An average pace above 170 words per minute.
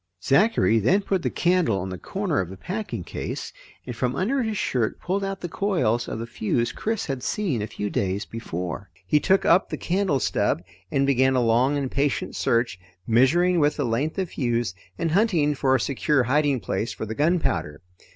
Yes: average, 200 wpm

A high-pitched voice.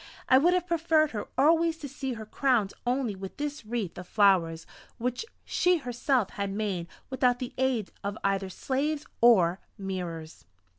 Yes: high, 240 Hz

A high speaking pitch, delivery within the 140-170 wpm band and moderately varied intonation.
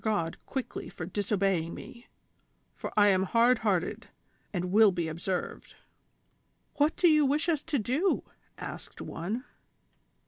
No: high, 210 Hz; average, 160 wpm; wide, 6.6 semitones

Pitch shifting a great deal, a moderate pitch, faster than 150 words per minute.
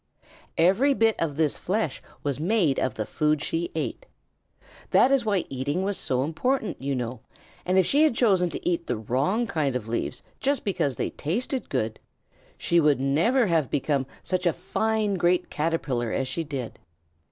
Yes: wide, 7.2 semitones; medium, 165 Hz; average, 175 wpm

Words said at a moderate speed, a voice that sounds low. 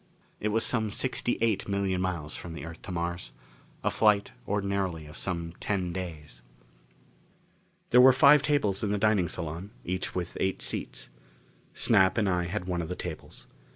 Yes: average, 170 wpm; very low, 95 Hz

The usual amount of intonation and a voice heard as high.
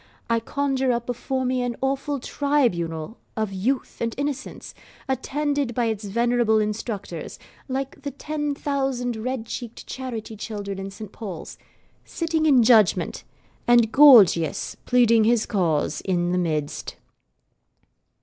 Yes: average, 4.2 semitones; high, 240 Hz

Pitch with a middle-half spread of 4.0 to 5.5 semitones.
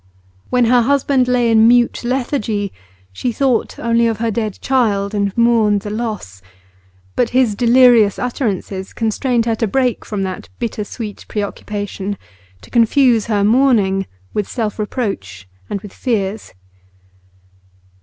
No: average, 3.1 semitones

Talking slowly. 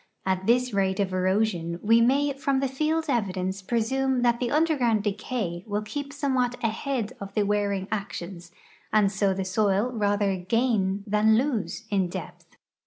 No: average, 160 wpm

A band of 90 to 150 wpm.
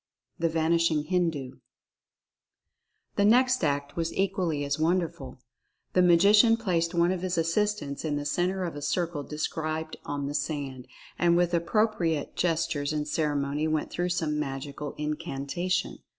Yes: average, 145 wpm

